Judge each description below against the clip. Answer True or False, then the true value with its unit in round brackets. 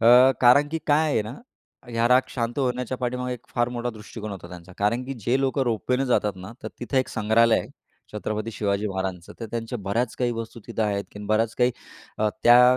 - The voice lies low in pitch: True (115 Hz)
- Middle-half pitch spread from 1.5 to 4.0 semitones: True (2.8 semitones)